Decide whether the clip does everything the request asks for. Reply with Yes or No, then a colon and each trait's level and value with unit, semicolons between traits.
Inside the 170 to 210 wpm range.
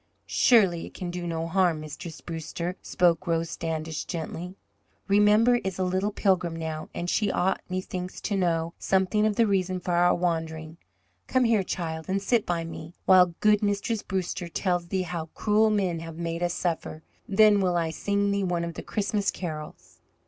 Yes: average, 180 wpm